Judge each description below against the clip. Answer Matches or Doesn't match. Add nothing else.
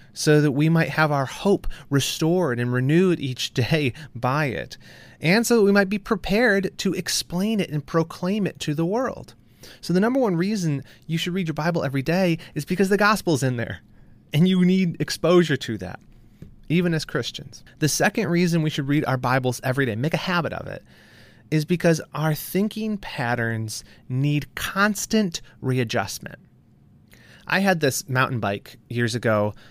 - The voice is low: Doesn't match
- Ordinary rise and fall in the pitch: Doesn't match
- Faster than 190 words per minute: Doesn't match